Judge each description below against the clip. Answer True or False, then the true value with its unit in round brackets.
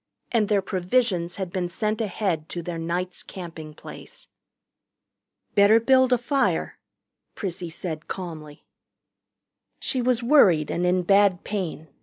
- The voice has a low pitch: False (185 Hz)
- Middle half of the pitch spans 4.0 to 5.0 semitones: True (4.3 semitones)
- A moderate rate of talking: False (130 wpm)